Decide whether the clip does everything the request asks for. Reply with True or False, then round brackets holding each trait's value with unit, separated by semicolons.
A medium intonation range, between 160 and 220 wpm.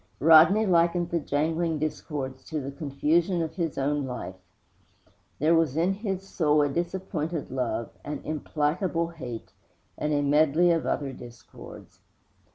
False (3.0 semitones; 140 wpm)